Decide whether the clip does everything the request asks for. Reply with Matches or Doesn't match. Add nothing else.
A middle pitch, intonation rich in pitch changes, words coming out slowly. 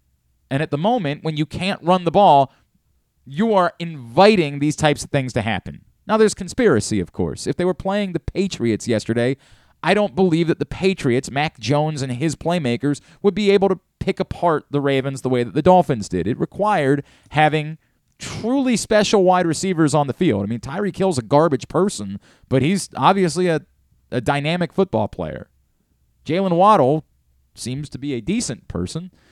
Doesn't match